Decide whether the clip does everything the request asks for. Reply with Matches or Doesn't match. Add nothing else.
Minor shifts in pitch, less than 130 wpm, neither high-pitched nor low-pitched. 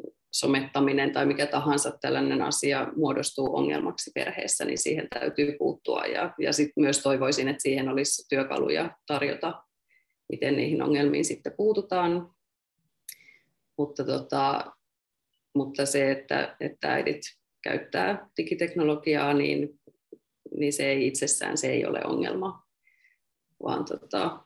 Matches